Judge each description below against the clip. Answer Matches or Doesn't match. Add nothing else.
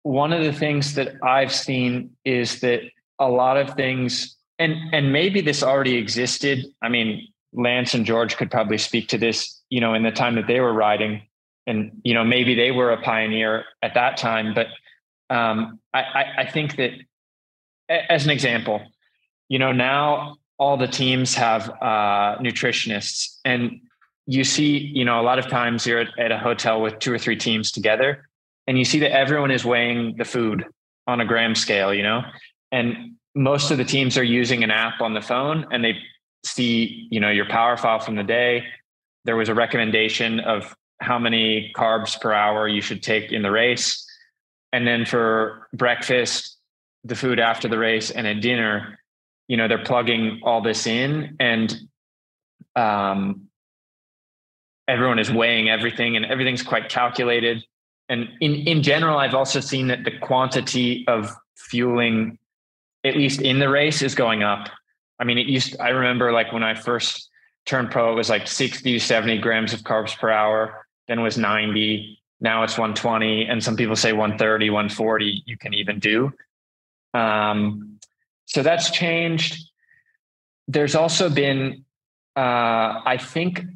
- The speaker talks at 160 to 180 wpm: Matches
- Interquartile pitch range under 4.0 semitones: Matches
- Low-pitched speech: Matches